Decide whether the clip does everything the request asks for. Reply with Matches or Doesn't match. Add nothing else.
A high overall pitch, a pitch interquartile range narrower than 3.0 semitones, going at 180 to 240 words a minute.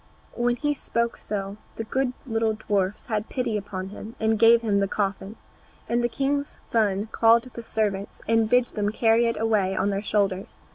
Matches